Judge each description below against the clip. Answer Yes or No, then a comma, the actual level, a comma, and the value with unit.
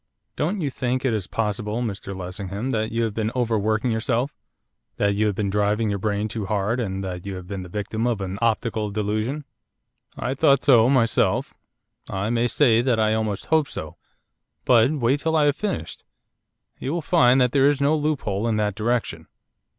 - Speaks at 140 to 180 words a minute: No, average, 190 wpm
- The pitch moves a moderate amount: Yes, average, 3.9 semitones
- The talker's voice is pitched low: Yes, low, 110 Hz